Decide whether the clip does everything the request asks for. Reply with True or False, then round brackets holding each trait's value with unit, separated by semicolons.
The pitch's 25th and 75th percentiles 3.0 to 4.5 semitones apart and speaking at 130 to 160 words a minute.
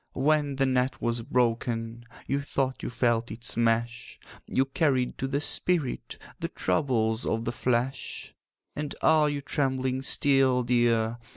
False (2.6 semitones; 145 wpm)